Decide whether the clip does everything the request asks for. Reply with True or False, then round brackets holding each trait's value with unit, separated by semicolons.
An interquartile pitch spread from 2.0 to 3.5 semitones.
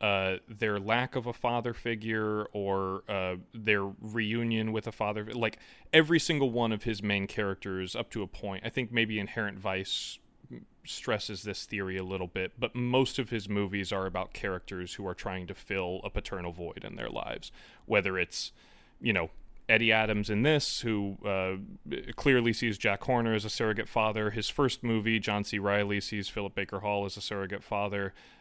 True (2.7 semitones)